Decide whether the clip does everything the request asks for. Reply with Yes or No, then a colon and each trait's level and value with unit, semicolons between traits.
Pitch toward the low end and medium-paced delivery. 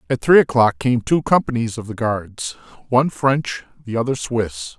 Yes: low, 120 Hz; average, 175 wpm